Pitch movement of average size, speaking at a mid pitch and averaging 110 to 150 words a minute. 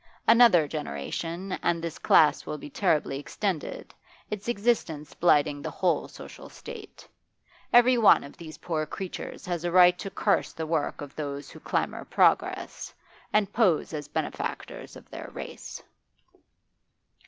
Yes: average, 4.9 semitones; medium, 170 Hz; average, 140 wpm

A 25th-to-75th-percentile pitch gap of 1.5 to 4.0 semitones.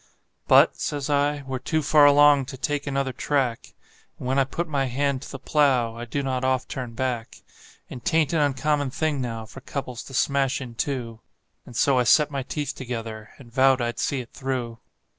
Yes: narrow, 2.6 semitones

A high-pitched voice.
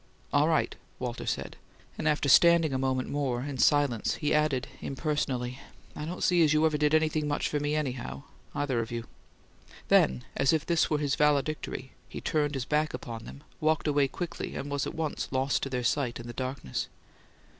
No: medium, 145 Hz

